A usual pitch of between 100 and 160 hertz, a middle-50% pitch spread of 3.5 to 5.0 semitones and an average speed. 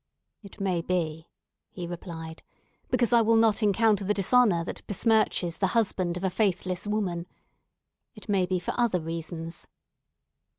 No: medium, 185 Hz; average, 3.8 semitones; average, 145 wpm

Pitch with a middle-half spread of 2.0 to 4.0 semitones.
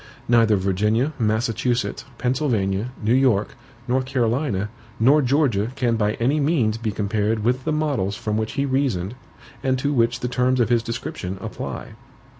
Yes: average, 3.5 semitones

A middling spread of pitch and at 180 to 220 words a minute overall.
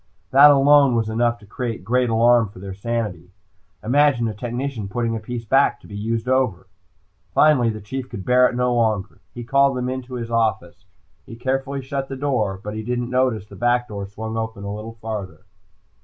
Yes: average, 3.0 semitones; average, 200 wpm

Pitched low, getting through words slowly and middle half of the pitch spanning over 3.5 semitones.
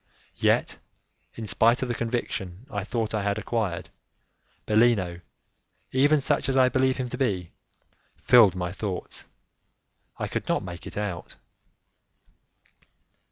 Yes: low, 110 Hz; slow, 130 wpm; average, 4.7 semitones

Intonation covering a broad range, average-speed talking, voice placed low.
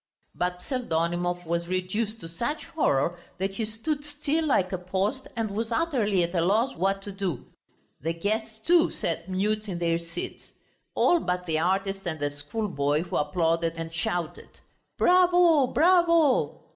No: wide, 5.7 semitones; average, 160 wpm; high, 190 Hz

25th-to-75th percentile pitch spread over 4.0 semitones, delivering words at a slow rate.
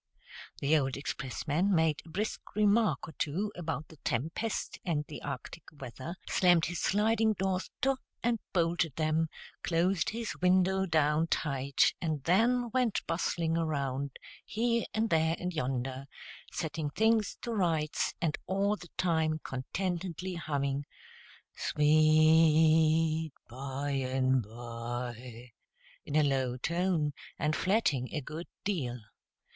Yes: average, 4.8 semitones; slow, 125 wpm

